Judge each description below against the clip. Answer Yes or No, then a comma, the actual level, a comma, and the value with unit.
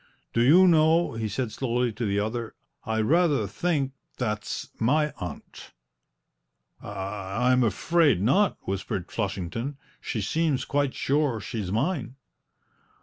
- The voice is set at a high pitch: No, low, 120 Hz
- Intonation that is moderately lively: No, wide, 5.7 semitones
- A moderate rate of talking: No, slow, 125 wpm